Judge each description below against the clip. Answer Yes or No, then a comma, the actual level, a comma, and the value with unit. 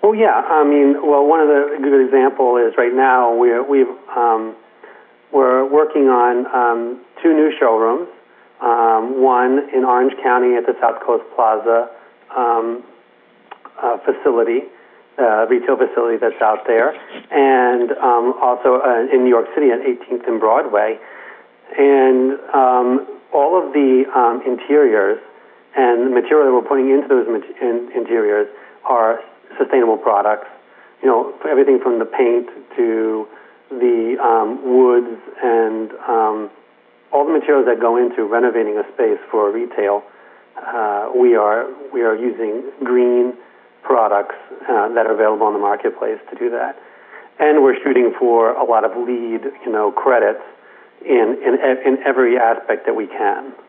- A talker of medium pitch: Yes, medium, 155 Hz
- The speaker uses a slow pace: No, average, 150 wpm